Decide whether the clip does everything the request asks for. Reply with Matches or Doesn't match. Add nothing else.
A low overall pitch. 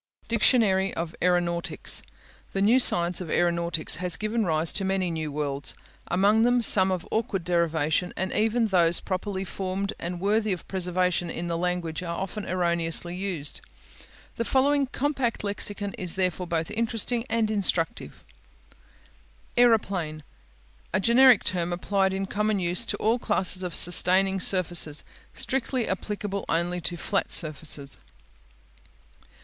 Doesn't match